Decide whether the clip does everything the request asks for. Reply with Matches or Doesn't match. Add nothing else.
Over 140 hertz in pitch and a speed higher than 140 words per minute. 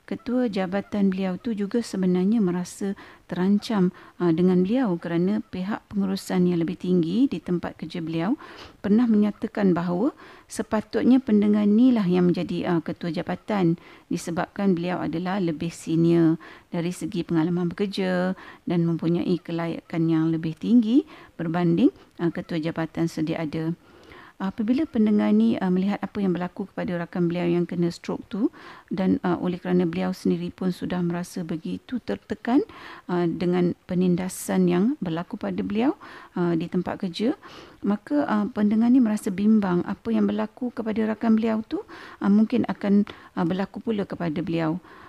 Matches